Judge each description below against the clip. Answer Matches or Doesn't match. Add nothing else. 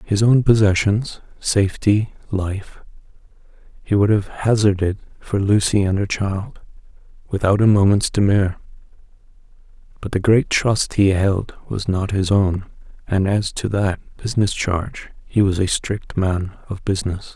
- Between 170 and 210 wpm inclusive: Doesn't match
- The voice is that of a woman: Doesn't match